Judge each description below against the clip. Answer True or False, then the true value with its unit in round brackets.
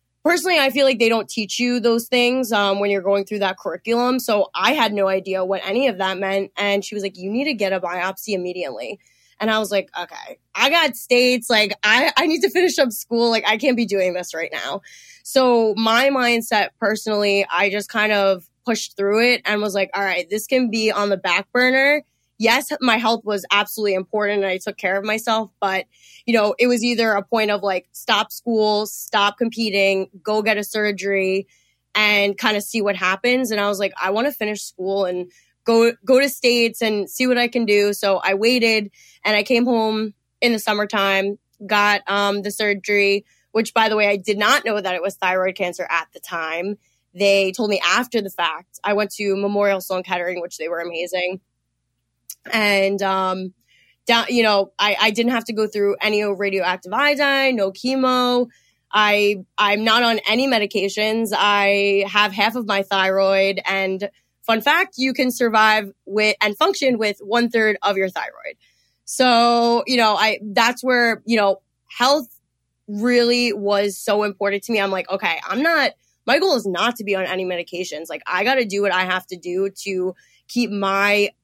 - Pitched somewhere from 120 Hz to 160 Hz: False (210 Hz)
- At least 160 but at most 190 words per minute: False (200 wpm)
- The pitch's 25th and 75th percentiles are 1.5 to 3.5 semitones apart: True (3.0 semitones)